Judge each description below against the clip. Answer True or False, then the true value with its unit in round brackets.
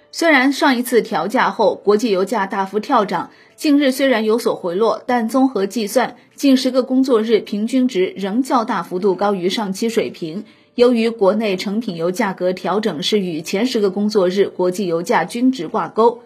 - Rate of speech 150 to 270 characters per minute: False (280 characters per minute)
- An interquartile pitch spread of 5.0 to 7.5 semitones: False (4.4 semitones)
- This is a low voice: False (220 Hz)